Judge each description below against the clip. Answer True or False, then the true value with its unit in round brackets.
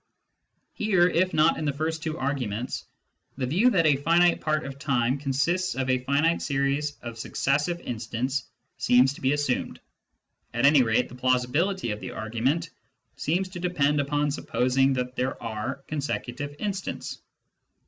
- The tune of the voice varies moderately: True (4.0 semitones)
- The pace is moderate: True (155 wpm)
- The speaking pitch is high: False (140 Hz)